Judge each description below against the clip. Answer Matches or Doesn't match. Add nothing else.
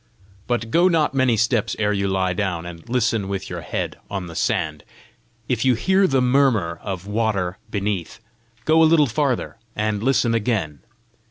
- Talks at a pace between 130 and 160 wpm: Doesn't match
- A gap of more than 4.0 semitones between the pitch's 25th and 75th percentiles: Matches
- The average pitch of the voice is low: Matches